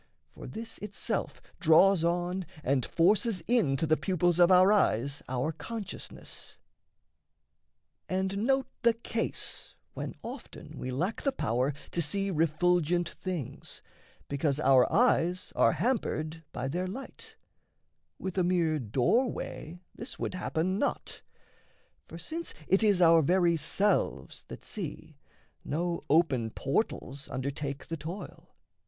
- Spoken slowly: Yes, slow, 125 wpm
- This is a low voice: No, medium, 175 Hz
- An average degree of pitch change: Yes, average, 4.8 semitones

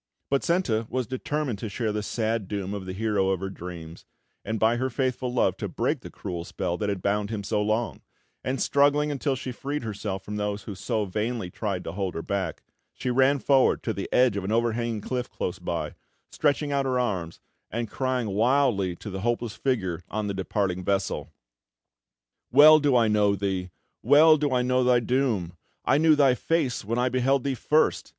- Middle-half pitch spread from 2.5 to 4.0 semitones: No, average, 4.5 semitones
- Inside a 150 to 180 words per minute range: No, average, 200 wpm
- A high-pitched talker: No, low, 115 Hz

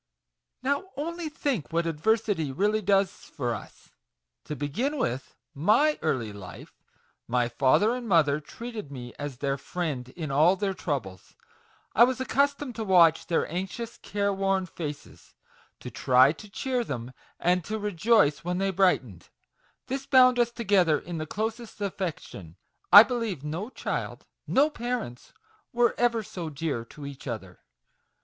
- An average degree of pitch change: No, wide, 8.1 semitones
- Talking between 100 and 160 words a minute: Yes, average, 150 wpm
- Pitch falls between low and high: Yes, medium, 180 Hz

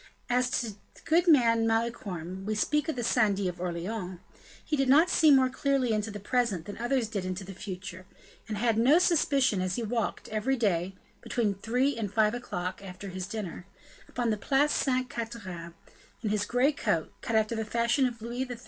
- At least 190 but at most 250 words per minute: Yes, average, 195 wpm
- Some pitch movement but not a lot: Yes, average, 4.4 semitones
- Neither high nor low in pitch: No, high, 225 Hz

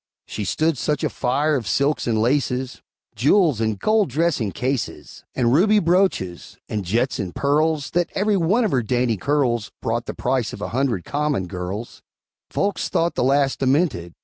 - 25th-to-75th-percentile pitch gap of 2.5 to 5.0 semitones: No, wide, 5.5 semitones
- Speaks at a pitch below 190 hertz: Yes, low, 135 Hz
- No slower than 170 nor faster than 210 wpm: Yes, average, 175 wpm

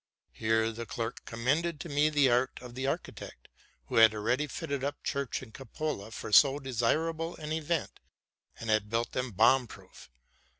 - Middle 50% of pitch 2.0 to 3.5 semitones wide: No, average, 4.5 semitones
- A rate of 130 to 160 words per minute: No, average, 175 wpm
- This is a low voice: Yes, low, 130 Hz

